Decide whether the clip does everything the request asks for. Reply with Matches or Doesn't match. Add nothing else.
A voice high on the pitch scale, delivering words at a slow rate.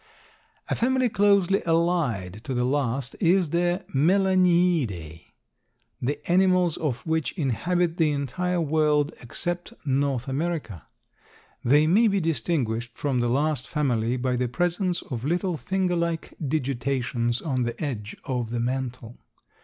Doesn't match